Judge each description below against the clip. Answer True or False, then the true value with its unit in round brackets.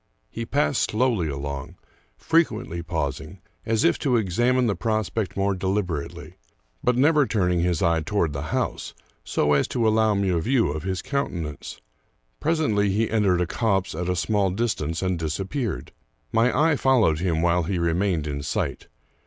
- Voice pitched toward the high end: False (95 Hz)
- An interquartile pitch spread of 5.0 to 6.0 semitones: True (5.4 semitones)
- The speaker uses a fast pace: False (170 wpm)